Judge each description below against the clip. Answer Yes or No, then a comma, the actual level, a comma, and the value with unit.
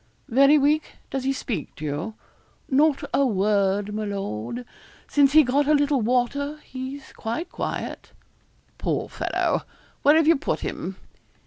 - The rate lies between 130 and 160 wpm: Yes, average, 145 wpm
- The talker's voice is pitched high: Yes, very high, 265 Hz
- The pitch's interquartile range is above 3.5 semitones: Yes, average, 5.3 semitones